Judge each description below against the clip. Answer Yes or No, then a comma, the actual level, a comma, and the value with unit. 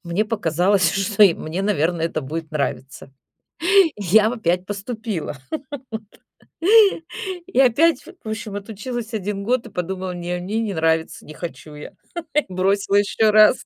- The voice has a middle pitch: No, high, 195 Hz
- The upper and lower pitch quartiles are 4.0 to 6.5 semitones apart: Yes, average, 4.3 semitones